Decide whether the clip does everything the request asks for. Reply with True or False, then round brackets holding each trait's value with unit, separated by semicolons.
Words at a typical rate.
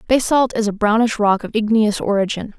True (185 wpm)